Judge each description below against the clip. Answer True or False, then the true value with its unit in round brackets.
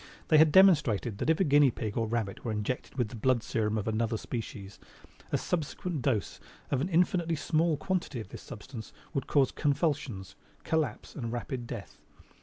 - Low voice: True (130 Hz)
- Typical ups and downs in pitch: False (5.8 semitones)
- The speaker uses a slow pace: False (180 wpm)